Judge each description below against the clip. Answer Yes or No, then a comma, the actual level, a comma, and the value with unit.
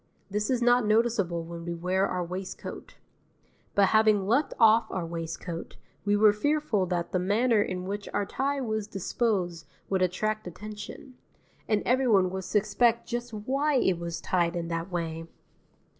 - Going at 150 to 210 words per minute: Yes, average, 160 wpm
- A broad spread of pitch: No, average, 4.1 semitones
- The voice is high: Yes, high, 205 Hz